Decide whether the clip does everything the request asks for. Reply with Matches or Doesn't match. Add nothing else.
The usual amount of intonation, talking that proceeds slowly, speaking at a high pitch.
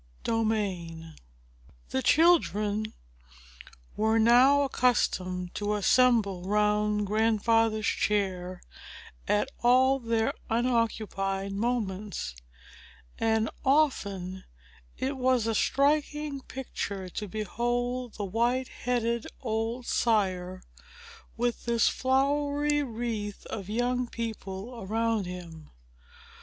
Matches